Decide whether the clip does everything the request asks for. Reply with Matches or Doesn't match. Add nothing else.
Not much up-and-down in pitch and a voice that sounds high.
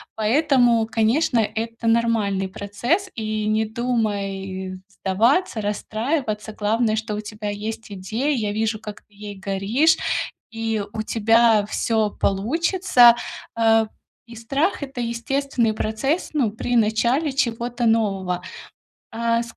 Matches